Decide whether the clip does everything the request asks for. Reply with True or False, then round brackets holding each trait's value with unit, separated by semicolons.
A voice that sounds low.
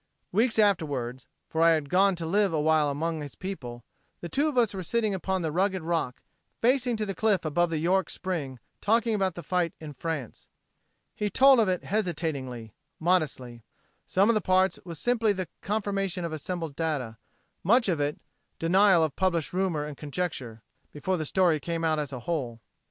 False (170 Hz)